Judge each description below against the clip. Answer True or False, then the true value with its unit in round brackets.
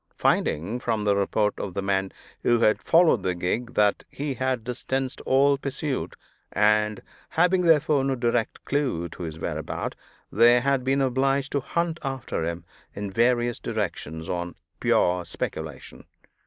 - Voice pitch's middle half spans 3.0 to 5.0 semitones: False (5.6 semitones)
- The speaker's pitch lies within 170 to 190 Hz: False (120 Hz)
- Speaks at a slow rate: False (150 wpm)